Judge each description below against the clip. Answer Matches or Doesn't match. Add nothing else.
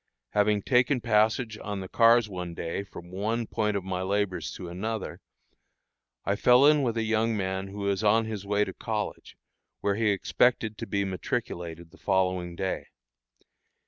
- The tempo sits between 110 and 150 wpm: Doesn't match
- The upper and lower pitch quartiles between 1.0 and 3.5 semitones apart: Matches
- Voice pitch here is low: Matches